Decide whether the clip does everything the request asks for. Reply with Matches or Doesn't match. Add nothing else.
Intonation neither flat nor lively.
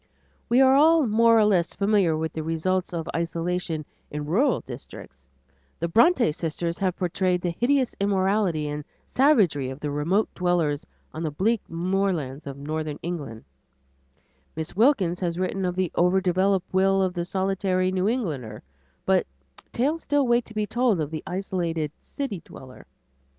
Matches